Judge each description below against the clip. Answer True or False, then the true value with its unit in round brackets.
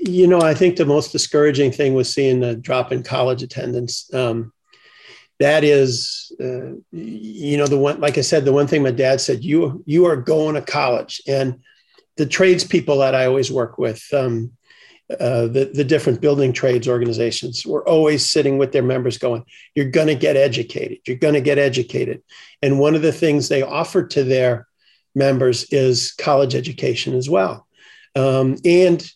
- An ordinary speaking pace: True (185 wpm)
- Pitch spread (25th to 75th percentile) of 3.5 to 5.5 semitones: False (3.0 semitones)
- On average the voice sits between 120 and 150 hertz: True (135 Hz)